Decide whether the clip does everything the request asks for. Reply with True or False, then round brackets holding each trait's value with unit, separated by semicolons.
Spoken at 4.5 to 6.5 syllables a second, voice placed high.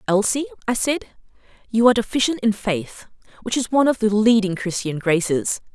True (5.6 syllables/s; 215 Hz)